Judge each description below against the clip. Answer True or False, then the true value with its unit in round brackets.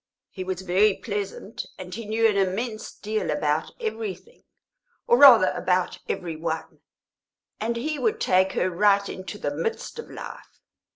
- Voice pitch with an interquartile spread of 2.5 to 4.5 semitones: True (3.4 semitones)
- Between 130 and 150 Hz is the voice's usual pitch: False (200 Hz)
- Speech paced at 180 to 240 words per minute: False (155 wpm)